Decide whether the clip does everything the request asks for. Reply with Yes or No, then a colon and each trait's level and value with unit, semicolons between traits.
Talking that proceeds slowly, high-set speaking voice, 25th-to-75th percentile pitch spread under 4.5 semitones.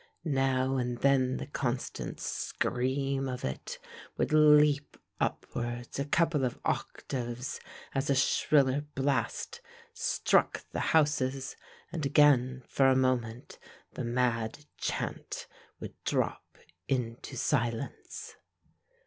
No: slow, 105 wpm; low, 135 Hz; narrow, 2.4 semitones